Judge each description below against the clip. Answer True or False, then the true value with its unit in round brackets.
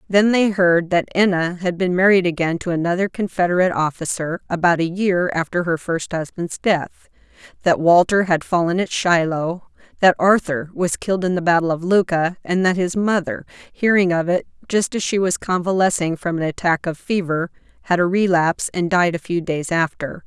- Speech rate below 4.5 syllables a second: False (5.1 syllables/s)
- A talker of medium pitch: True (175 Hz)